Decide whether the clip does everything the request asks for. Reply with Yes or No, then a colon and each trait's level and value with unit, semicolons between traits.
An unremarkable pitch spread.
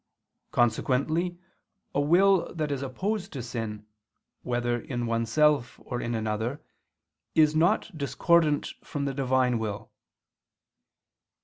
Yes: average, 4.6 semitones